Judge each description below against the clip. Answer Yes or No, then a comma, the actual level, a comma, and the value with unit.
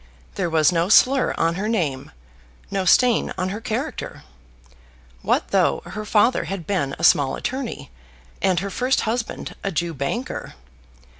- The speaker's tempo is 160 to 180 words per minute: No, average, 150 wpm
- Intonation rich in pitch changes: Yes, wide, 5.7 semitones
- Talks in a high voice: Yes, high, 195 Hz